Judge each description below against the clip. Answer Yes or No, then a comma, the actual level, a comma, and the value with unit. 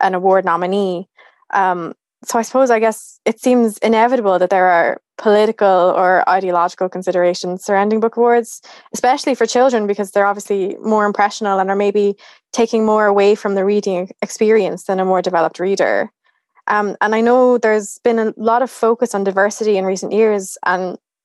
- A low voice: No, high, 205 Hz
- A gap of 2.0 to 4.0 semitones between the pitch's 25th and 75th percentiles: Yes, average, 3.2 semitones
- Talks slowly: No, average, 170 wpm